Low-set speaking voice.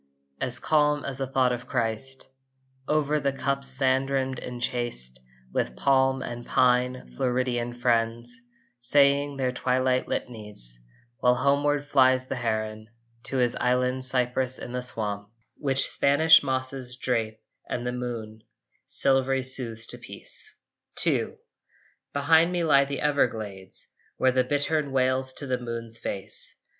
Yes: low, 130 Hz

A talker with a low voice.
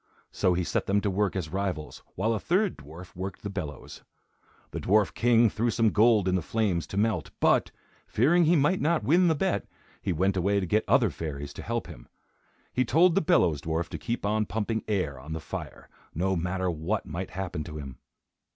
Yes: very low, 95 Hz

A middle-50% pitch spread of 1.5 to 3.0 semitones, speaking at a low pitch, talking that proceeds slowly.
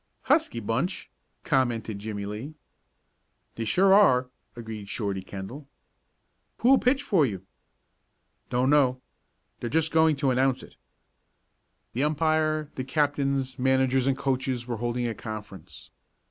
No: average, 4.6 semitones; low, 130 Hz; slow, 125 wpm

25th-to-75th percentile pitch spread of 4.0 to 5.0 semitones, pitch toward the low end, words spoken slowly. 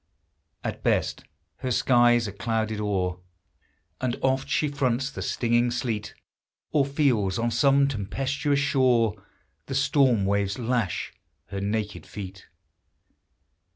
Yes: average, 4.4 semitones; low, 120 Hz; slow, 120 wpm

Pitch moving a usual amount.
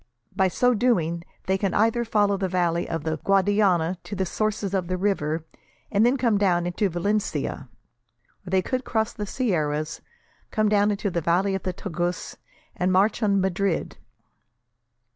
Yes: average, 3.2 semitones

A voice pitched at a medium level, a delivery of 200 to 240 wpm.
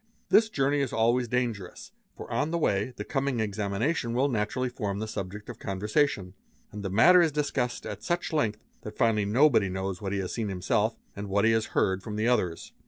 No: low, 110 Hz; fast, 205 wpm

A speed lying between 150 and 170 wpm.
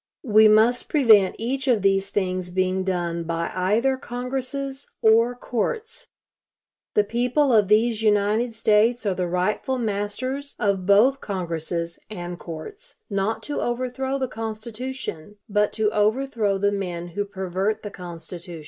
No: average, 140 wpm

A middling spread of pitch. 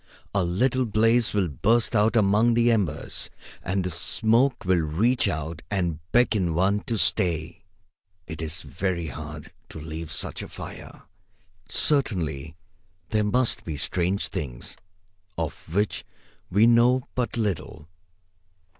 No: wide, 5.9 semitones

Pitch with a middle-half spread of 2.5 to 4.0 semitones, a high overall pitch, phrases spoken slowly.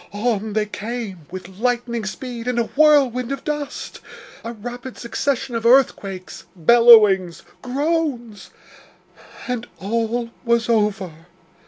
Yes: average, 3.1 semitones; high, 235 Hz; slow, 115 wpm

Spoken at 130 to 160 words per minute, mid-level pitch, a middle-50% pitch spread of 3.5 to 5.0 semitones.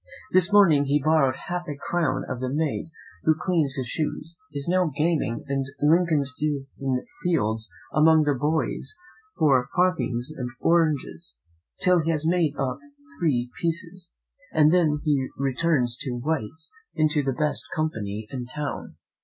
Yes: average, 150 wpm; medium, 150 Hz; average, 3.9 semitones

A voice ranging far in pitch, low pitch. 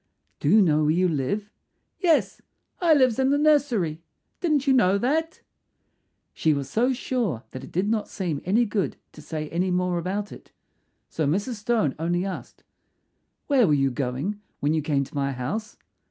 No: wide, 7.8 semitones; high, 190 Hz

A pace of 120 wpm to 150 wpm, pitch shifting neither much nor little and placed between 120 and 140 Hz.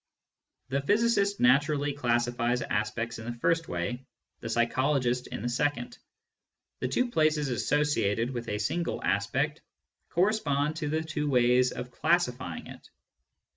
Yes: slow, 135 wpm; average, 4.4 semitones; low, 135 Hz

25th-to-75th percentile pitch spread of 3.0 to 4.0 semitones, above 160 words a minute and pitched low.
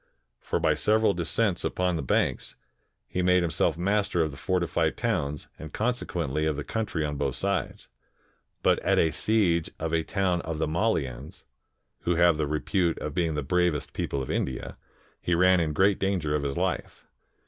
Yes: average, 3.4 semitones; average, 180 wpm; very low, 85 Hz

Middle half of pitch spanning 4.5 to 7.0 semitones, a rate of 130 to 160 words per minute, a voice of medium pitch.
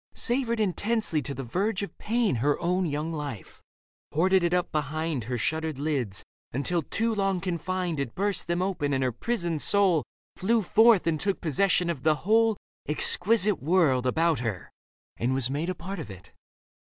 No: average, 5.3 semitones; average, 175 wpm; medium, 170 Hz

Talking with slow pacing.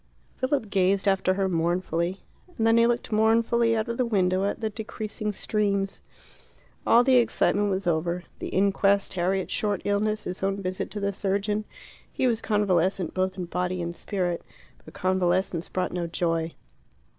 No: average, 165 wpm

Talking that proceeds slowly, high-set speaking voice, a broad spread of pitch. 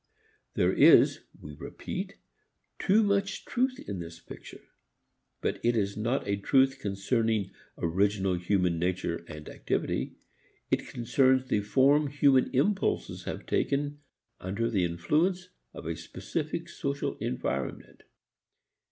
No: slow, 120 wpm; low, 110 Hz; wide, 7.4 semitones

